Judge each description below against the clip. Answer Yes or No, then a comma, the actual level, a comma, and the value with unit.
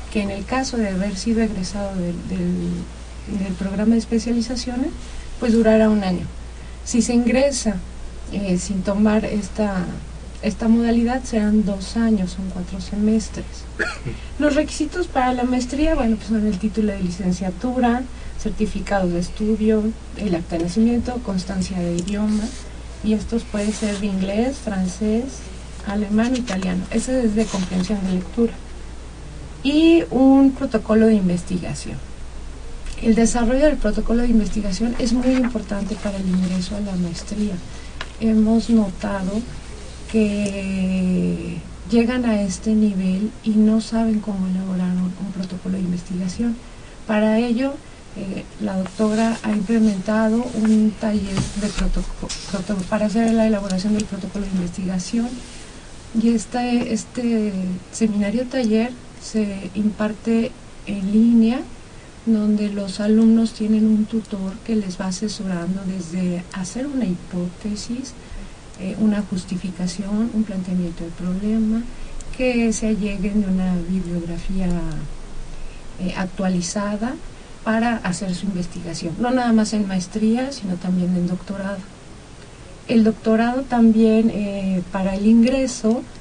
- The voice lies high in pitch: Yes, high, 210 Hz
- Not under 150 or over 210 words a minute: No, slow, 125 wpm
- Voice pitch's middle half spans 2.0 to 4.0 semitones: Yes, average, 3.3 semitones